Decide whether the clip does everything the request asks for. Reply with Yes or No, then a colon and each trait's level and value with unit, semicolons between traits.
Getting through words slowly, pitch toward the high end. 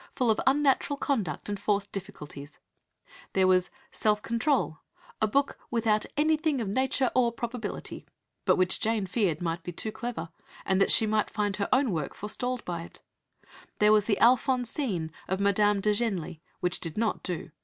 No: average, 170 wpm; high, 210 Hz